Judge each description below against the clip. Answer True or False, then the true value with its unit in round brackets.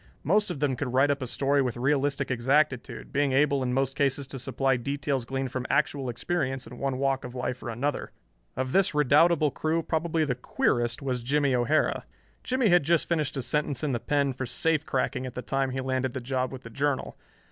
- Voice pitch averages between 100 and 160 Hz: True (135 Hz)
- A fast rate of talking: True (210 wpm)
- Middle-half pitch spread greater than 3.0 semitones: False (2.4 semitones)